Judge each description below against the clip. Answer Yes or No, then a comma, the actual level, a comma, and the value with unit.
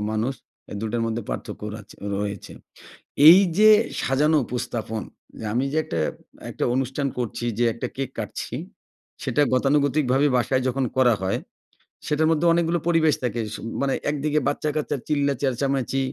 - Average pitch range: Yes, average, 3.9 semitones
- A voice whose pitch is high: No, low, 135 Hz